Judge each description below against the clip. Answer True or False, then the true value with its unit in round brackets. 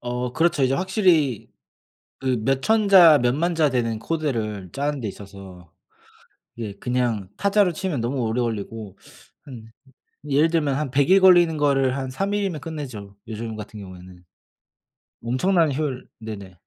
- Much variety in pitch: True (6.3 semitones)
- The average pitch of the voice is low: True (130 Hz)